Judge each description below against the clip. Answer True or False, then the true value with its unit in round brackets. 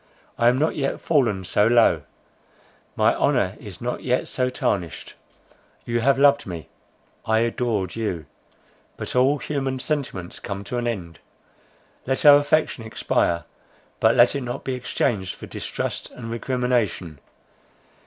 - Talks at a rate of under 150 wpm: True (140 wpm)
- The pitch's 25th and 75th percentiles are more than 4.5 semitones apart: True (5.1 semitones)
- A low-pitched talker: True (120 Hz)